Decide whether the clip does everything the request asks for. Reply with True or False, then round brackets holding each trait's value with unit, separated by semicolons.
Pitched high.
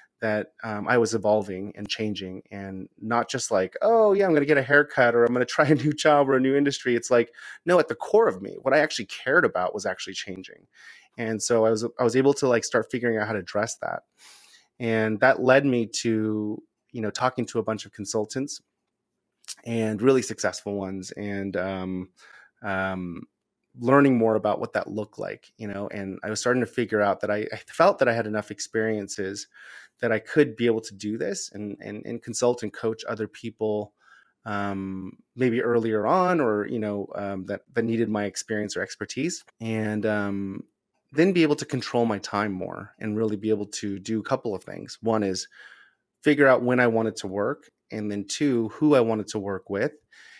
False (110 Hz)